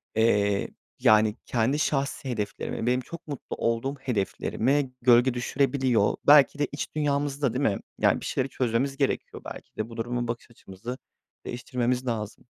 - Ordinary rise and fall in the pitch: Yes, average, 3.2 semitones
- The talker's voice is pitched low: Yes, low, 125 Hz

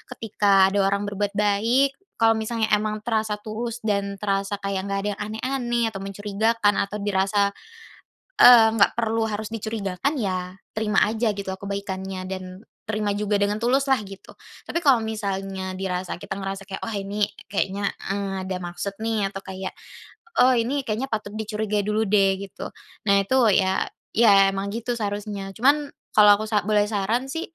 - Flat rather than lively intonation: Yes, narrow, 2.1 semitones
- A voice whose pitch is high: Yes, high, 205 Hz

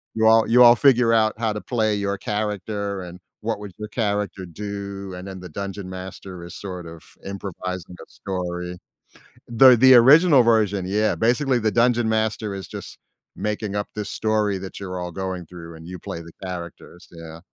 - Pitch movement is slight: No, average, 3.2 semitones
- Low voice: Yes, low, 100 Hz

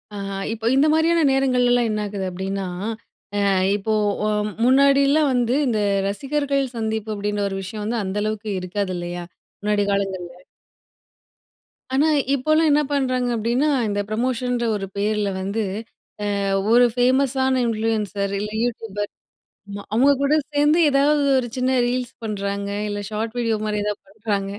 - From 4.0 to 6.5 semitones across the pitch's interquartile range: Yes, average, 4.3 semitones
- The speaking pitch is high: Yes, high, 225 Hz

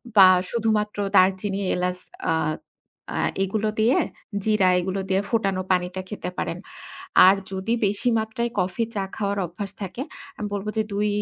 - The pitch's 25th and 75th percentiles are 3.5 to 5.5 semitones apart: No, narrow, 2.5 semitones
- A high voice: Yes, high, 200 Hz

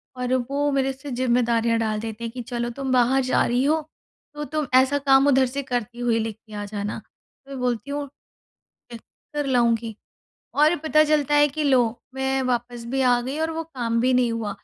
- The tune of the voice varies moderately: Yes, average, 3.1 semitones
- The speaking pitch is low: No, very high, 250 Hz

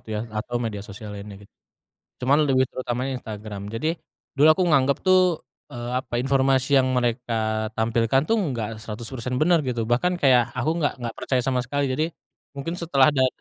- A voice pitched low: Yes, low, 125 Hz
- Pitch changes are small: No, average, 3.3 semitones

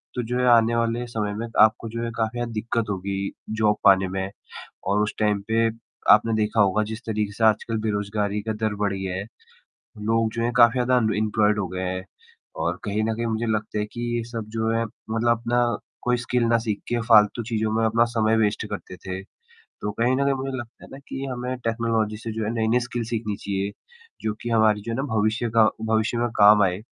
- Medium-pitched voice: No, low, 110 Hz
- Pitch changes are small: Yes, narrow, 2.0 semitones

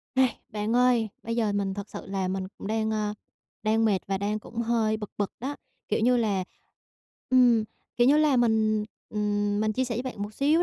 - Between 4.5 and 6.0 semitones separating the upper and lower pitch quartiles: No, average, 2.7 semitones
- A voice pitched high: Yes, high, 220 Hz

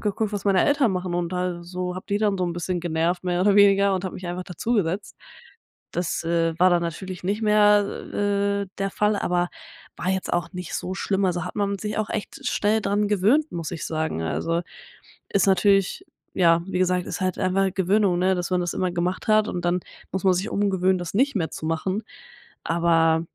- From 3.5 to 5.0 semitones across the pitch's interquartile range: No, narrow, 2.5 semitones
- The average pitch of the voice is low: No, medium, 185 Hz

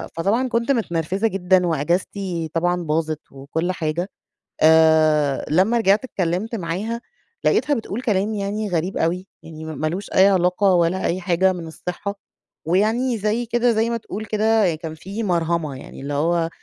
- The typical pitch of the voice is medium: Yes, medium, 180 Hz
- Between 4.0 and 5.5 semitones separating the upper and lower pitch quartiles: Yes, average, 4.5 semitones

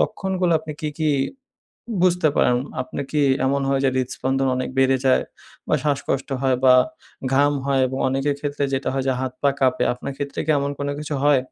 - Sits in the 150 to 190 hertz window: No, medium, 140 Hz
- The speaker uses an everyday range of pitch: No, narrow, 1.8 semitones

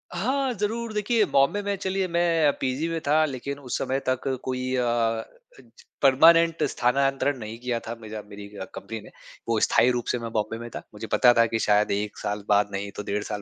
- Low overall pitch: Yes, low, 130 Hz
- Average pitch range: No, wide, 6.9 semitones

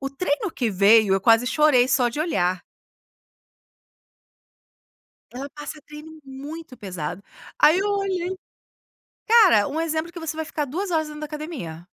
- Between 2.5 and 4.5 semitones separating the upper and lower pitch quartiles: No, average, 5.2 semitones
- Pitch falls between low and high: No, very high, 300 Hz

